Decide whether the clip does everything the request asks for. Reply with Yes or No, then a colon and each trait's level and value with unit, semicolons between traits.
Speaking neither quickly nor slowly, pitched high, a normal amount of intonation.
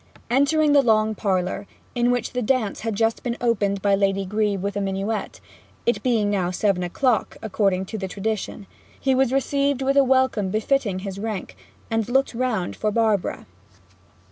Yes: average, 170 wpm; high, 220 Hz; average, 4.0 semitones